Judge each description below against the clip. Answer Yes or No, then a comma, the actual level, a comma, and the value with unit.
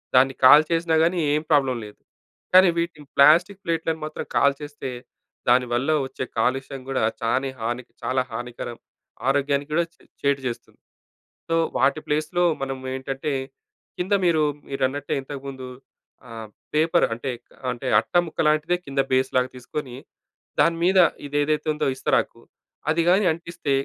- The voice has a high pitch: No, medium, 140 Hz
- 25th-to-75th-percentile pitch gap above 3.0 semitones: Yes, average, 3.5 semitones